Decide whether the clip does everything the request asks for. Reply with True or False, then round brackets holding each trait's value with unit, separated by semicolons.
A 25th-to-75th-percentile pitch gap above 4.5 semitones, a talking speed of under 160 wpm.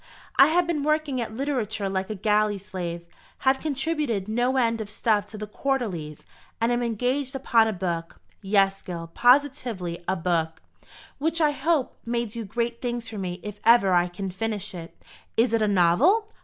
False (5.3 semitones; 180 wpm)